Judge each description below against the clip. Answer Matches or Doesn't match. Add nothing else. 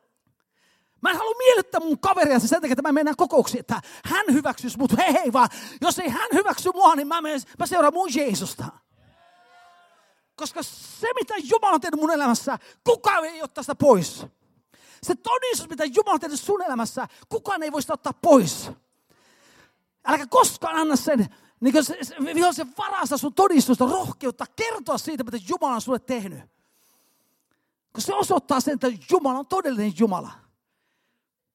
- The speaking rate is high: Matches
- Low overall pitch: Doesn't match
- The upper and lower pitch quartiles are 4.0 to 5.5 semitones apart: Matches